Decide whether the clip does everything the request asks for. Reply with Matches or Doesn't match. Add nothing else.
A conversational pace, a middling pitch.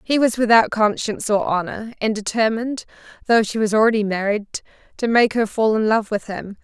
Doesn't match